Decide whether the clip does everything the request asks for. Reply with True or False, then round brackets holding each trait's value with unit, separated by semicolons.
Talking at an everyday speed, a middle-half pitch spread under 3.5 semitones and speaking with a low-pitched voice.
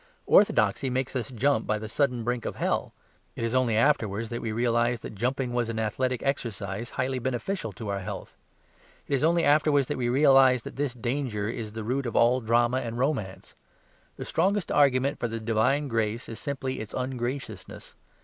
True (190 wpm; 3.1 semitones; 120 Hz)